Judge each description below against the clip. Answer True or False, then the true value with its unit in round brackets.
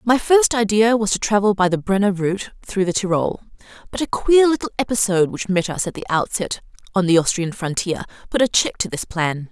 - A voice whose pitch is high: True (200 Hz)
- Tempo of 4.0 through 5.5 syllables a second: False (5.7 syllables/s)